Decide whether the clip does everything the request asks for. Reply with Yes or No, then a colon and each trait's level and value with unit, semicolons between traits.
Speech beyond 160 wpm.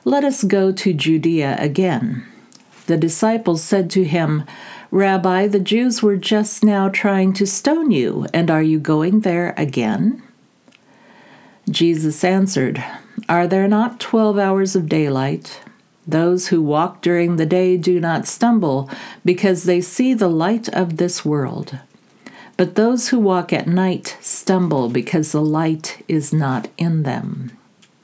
No: average, 145 wpm